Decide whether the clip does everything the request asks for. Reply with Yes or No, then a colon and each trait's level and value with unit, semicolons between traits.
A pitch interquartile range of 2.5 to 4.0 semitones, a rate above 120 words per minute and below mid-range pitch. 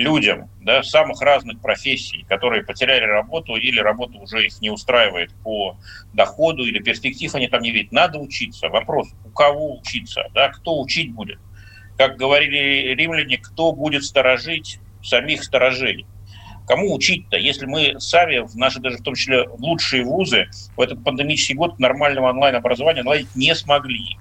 No: average, 5.3 semitones; average, 155 wpm; low, 125 Hz